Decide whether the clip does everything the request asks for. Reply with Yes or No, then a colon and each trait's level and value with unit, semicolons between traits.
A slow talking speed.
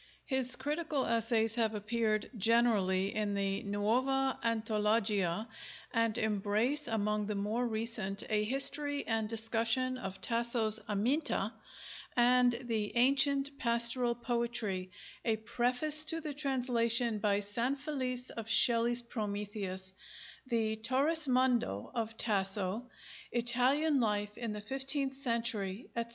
Yes: slow, 110 wpm